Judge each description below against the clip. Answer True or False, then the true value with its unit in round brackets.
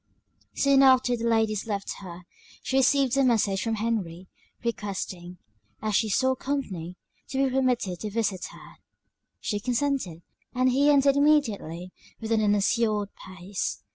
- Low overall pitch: False (225 Hz)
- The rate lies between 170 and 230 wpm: False (140 wpm)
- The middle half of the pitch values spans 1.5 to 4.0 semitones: False (5.1 semitones)